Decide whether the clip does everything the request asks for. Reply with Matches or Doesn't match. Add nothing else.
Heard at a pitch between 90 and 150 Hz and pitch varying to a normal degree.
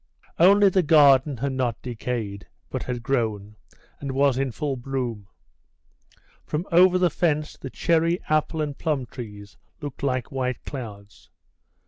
Matches